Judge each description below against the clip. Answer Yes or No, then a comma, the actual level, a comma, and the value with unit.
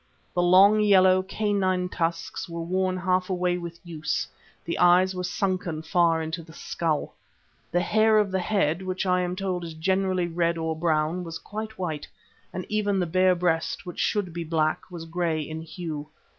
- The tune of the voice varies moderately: No, narrow, 2.2 semitones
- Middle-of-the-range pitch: Yes, medium, 180 Hz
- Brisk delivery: No, average, 180 wpm